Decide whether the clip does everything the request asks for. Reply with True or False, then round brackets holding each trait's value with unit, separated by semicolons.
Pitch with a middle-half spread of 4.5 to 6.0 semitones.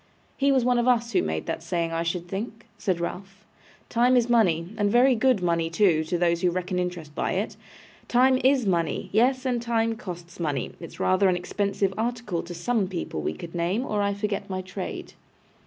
True (5.4 semitones)